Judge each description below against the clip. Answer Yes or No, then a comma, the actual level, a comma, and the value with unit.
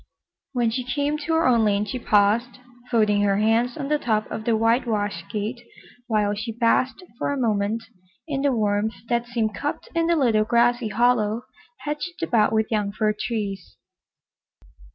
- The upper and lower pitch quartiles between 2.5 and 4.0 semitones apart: Yes, average, 3.0 semitones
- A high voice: Yes, high, 230 Hz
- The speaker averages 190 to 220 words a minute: No, average, 170 wpm